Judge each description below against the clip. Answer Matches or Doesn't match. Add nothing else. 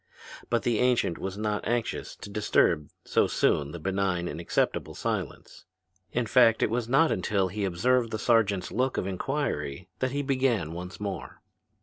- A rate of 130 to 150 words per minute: Doesn't match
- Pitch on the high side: Doesn't match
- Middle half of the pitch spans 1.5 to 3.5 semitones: Doesn't match